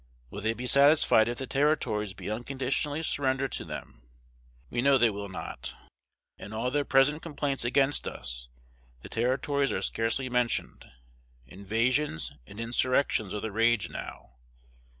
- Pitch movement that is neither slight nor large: Yes, average, 4.0 semitones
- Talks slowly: No, average, 145 wpm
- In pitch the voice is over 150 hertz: No, low, 125 Hz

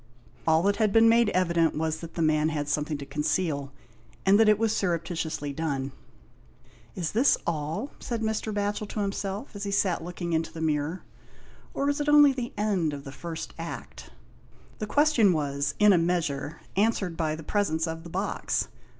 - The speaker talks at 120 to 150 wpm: No, average, 190 wpm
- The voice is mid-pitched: Yes, medium, 170 Hz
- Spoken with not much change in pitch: No, average, 4.9 semitones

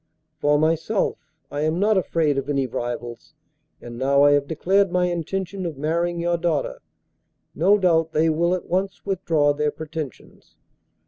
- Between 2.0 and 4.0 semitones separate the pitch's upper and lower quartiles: Yes, average, 3.7 semitones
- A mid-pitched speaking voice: Yes, medium, 165 Hz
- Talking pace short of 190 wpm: Yes, average, 155 wpm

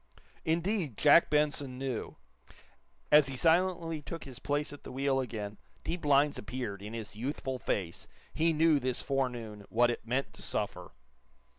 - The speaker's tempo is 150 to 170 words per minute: Yes, average, 155 wpm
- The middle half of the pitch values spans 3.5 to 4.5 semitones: Yes, average, 4.0 semitones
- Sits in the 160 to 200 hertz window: No, low, 135 Hz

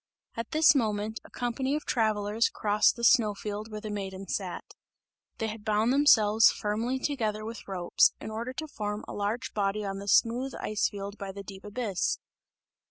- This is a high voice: Yes, high, 215 Hz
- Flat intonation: Yes, narrow, 2.3 semitones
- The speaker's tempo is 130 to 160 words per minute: No, average, 180 wpm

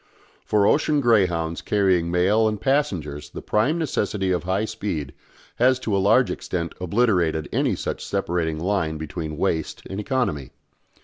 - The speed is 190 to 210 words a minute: No, average, 145 wpm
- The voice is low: Yes, very low, 95 Hz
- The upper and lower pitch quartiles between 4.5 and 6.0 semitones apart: Yes, average, 5.0 semitones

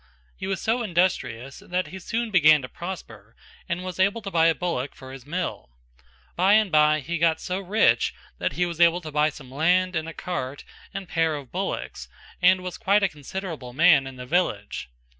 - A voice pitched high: No, medium, 170 Hz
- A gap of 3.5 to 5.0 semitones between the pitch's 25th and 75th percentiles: Yes, average, 3.9 semitones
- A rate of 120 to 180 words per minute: No, average, 200 wpm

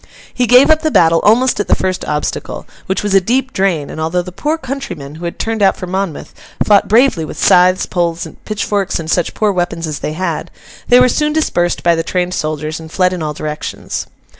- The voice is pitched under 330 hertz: Yes, medium, 185 Hz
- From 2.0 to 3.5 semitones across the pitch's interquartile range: No, average, 5.2 semitones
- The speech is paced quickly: Yes, fast, 215 wpm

